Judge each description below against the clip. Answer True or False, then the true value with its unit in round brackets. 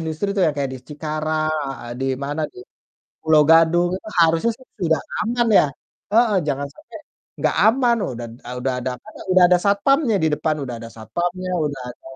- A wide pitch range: True (5.8 semitones)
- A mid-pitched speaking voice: True (160 Hz)